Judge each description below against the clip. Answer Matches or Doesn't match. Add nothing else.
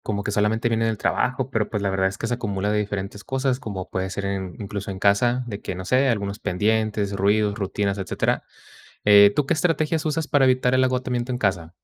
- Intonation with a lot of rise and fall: Doesn't match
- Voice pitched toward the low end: Matches